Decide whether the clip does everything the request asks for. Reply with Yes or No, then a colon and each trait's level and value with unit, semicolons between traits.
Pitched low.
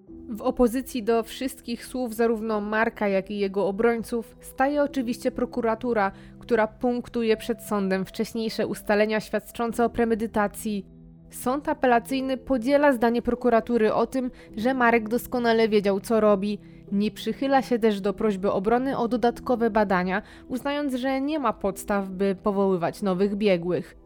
No: high, 225 Hz